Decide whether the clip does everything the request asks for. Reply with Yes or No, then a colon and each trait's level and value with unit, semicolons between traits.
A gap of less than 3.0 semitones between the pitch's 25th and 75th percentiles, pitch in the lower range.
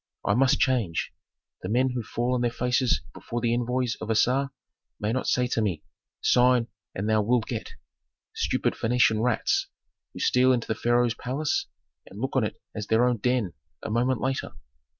Yes: narrow, 2.4 semitones; low, 120 Hz